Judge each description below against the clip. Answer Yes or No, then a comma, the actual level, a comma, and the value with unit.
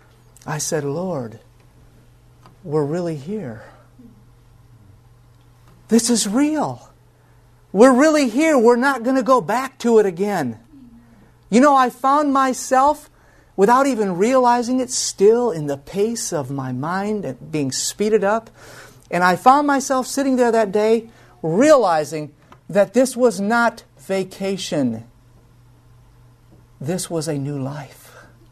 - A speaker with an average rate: No, slow, 125 wpm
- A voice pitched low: No, medium, 185 Hz